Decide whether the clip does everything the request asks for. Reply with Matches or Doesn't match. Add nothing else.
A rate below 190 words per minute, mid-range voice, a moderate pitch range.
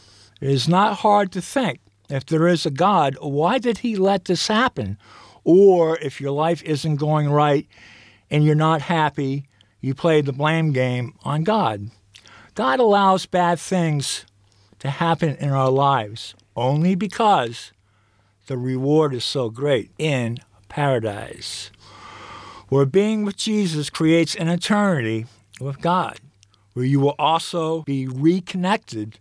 Doesn't match